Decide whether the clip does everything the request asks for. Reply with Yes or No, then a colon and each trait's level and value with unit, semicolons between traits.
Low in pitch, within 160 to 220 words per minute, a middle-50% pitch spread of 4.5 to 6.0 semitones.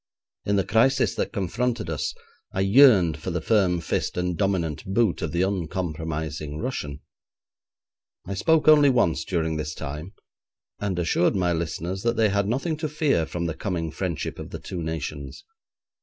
Yes: very low, 90 Hz; average, 165 wpm; average, 5.2 semitones